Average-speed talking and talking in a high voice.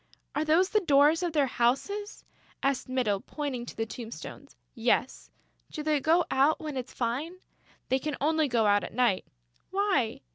Yes: average, 170 wpm; very high, 275 Hz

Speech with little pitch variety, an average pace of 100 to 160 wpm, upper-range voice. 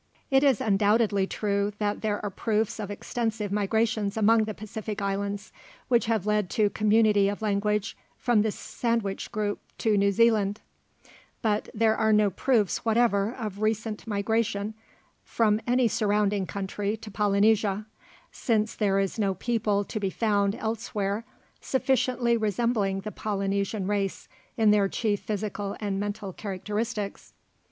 Yes: narrow, 1.8 semitones; average, 140 wpm; high, 210 Hz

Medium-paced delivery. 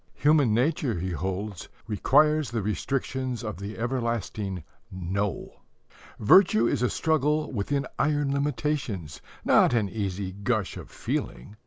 No: slow, 125 wpm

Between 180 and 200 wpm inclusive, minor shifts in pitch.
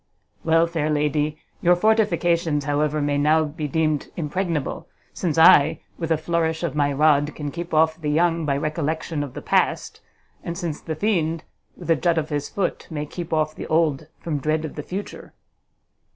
Yes: average, 185 wpm; narrow, 2.1 semitones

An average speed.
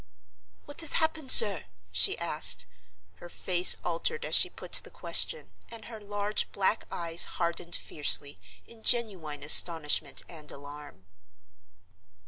No: slow, 125 wpm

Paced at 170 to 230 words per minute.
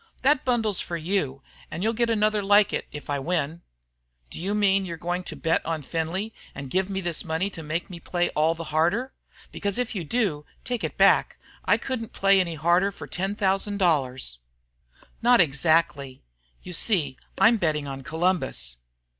Yes: average, 185 wpm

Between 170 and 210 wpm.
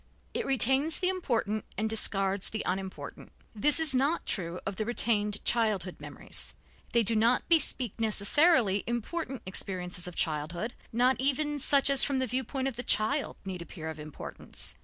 No: average, 160 wpm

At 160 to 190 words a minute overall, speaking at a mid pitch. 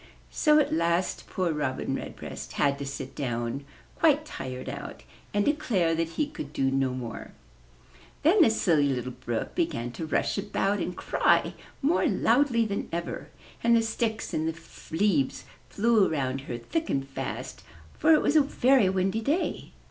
Yes: average, 165 wpm; medium, 180 Hz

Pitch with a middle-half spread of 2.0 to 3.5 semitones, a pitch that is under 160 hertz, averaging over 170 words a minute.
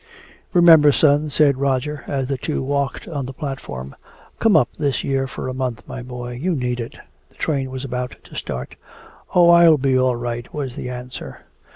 Yes: average, 2.9 semitones; low, 135 Hz; average, 190 wpm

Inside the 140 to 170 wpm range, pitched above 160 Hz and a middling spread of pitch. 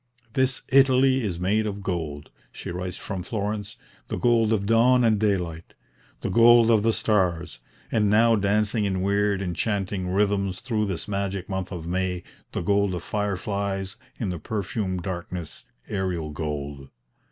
No: average, 150 wpm; low, 100 Hz; average, 3.1 semitones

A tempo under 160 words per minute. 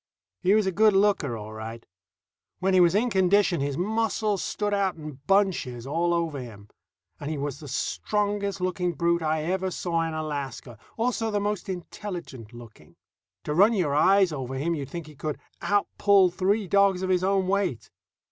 No: average, 180 wpm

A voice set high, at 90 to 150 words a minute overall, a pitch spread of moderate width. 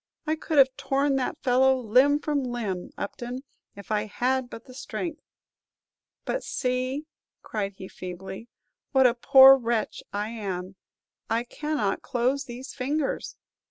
Yes: very high, 250 Hz; average, 140 wpm; average, 3.8 semitones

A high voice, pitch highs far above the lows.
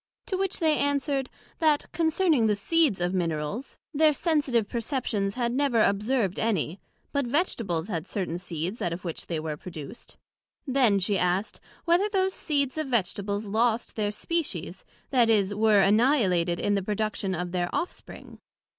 Yes: high, 215 Hz; wide, 7.2 semitones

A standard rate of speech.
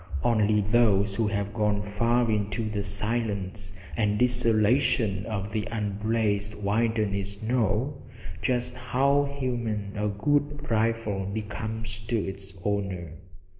No: slow, 115 wpm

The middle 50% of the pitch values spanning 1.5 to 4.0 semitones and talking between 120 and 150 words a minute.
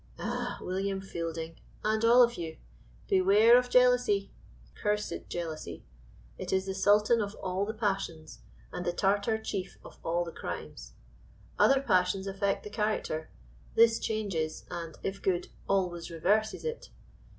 Yes: average, 3.7 semitones; average, 140 wpm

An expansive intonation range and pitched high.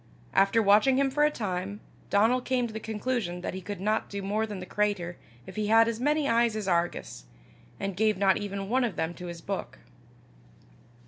No: average, 3.2 semitones; high, 210 Hz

